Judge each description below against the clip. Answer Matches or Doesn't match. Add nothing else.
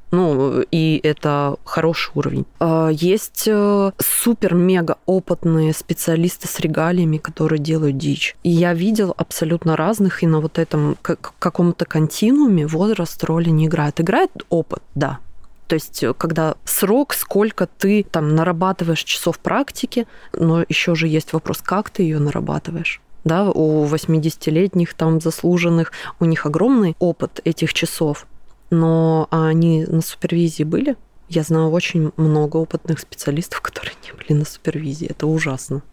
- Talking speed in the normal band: Matches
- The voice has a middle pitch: Matches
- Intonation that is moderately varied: Doesn't match